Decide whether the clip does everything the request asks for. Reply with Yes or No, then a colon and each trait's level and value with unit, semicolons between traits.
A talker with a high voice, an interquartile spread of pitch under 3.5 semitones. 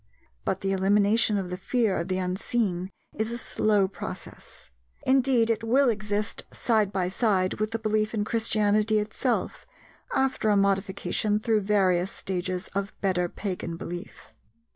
Yes: high, 205 Hz; average, 2.7 semitones